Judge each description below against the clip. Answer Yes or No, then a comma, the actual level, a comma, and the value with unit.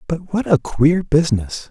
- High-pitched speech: No, medium, 150 Hz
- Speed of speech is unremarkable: Yes, average, 175 wpm